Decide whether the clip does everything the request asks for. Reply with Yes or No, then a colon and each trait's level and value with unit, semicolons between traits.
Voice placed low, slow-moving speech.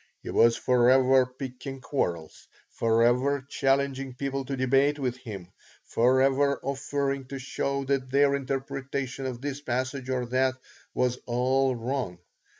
Yes: low, 130 Hz; slow, 130 wpm